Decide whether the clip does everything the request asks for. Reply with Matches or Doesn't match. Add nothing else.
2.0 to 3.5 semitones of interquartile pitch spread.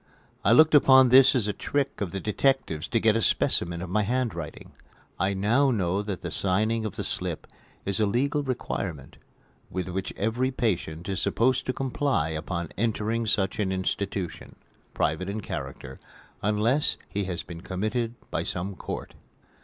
Doesn't match